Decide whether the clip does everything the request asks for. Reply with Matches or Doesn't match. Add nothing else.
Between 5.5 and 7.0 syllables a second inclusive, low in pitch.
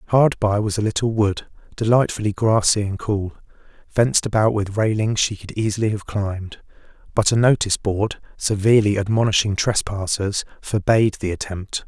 Doesn't match